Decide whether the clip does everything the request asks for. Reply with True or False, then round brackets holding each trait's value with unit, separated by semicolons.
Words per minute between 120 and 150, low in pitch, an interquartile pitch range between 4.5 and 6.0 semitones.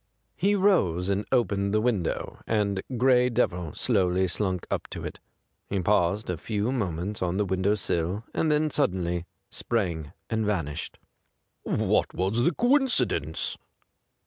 True (140 wpm; 100 Hz; 5.2 semitones)